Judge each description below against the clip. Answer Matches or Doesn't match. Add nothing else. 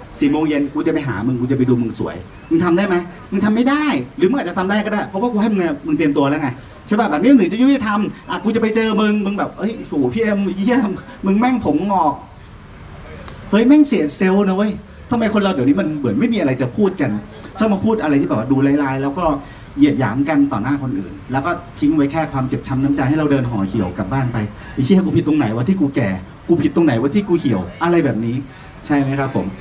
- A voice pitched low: Doesn't match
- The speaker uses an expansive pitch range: Matches